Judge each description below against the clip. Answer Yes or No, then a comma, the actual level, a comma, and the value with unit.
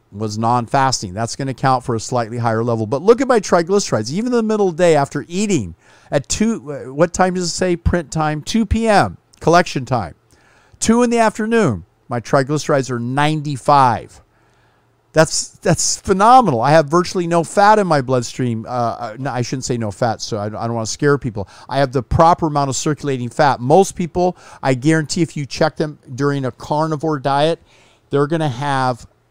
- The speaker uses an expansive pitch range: Yes, wide, 6.1 semitones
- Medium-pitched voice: Yes, medium, 145 Hz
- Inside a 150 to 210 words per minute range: Yes, average, 200 wpm